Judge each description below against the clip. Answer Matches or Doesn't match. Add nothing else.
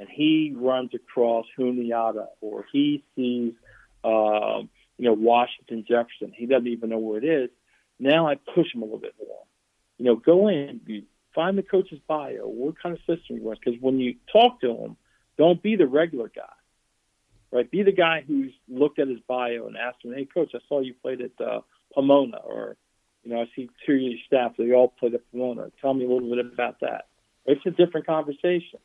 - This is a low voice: Matches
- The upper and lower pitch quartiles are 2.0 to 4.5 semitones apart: Doesn't match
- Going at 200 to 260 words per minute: Matches